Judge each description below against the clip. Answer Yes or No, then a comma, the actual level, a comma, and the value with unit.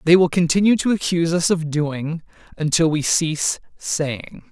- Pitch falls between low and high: Yes, medium, 165 Hz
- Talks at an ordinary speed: Yes, average, 160 wpm